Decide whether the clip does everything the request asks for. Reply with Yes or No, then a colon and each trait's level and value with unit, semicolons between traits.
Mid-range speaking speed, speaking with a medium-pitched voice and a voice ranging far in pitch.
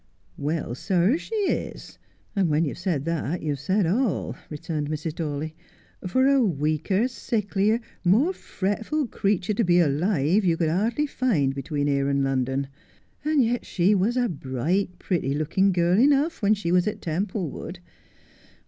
Yes: average, 160 wpm; medium, 180 Hz; wide, 5.8 semitones